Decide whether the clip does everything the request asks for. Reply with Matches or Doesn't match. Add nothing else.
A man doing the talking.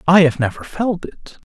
Matches